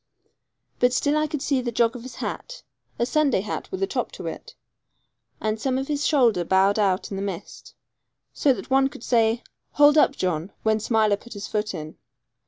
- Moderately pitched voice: No, high, 235 Hz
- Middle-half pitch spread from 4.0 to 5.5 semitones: Yes, average, 5.1 semitones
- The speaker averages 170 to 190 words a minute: No, average, 200 wpm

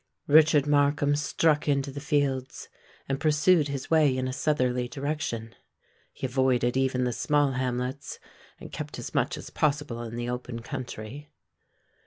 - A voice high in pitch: No, low, 135 Hz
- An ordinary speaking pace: Yes, average, 150 wpm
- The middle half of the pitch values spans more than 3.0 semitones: No, average, 2.7 semitones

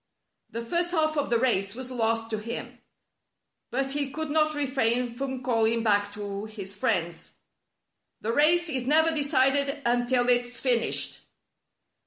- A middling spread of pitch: Yes, average, 3.9 semitones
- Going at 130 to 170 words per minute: Yes, average, 160 wpm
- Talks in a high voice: Yes, high, 245 Hz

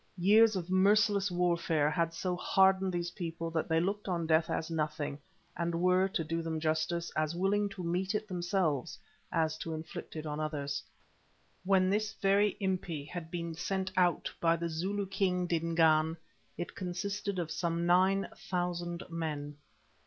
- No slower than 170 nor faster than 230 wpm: No, average, 160 wpm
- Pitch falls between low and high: Yes, medium, 175 Hz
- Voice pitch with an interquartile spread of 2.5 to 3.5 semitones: Yes, average, 2.8 semitones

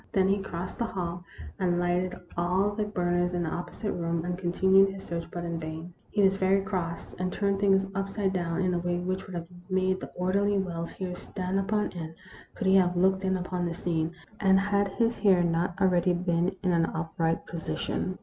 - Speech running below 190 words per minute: No, fast, 205 wpm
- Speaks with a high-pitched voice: No, medium, 180 Hz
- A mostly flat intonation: Yes, narrow, 1.8 semitones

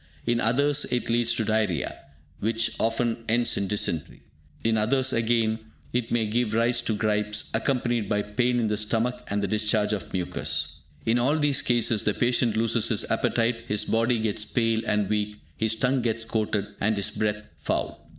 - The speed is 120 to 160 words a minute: No, average, 180 wpm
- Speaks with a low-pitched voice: Yes, low, 115 Hz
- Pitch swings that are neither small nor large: No, narrow, 2.1 semitones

